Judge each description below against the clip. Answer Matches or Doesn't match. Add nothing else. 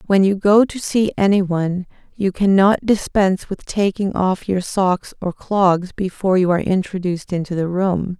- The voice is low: Doesn't match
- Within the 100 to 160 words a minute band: Doesn't match